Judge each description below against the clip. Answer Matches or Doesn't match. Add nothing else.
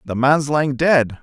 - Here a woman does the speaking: Doesn't match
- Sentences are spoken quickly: Doesn't match